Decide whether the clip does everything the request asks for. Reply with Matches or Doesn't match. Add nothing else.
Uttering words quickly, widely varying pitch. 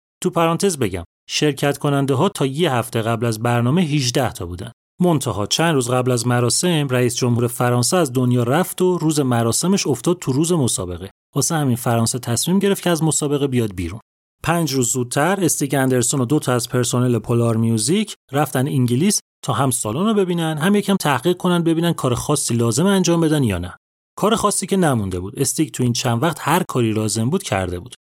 Matches